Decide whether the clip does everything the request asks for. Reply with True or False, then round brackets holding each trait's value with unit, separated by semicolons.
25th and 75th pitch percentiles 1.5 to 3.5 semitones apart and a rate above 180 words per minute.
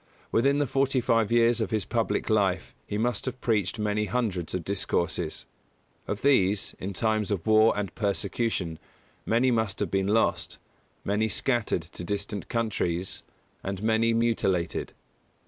False (3.1 semitones; 145 wpm)